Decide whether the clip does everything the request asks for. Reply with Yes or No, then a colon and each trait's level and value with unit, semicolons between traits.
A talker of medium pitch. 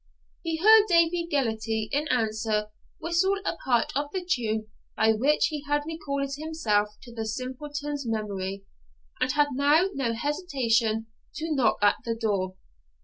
No: very high, 265 Hz